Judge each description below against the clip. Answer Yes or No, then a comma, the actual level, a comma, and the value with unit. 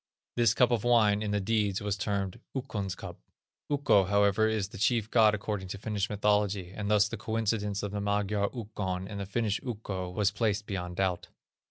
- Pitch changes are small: Yes, narrow, 1.8 semitones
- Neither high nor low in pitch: No, low, 105 Hz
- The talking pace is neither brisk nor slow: Yes, average, 190 wpm